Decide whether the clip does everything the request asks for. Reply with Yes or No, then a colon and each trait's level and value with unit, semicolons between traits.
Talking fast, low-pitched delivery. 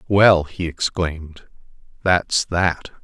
No: slow, 100 wpm; very low, 85 Hz